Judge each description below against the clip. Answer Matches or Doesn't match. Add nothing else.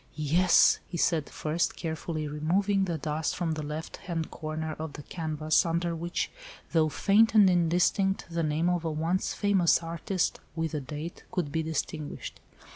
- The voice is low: Doesn't match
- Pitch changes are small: Matches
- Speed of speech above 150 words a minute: Matches